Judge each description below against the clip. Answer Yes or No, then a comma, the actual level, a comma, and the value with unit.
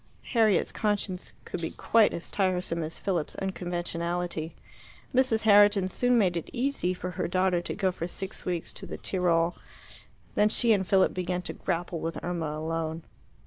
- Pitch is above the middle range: No, medium, 180 Hz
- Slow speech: No, average, 165 wpm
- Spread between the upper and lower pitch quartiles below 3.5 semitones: Yes, average, 3.0 semitones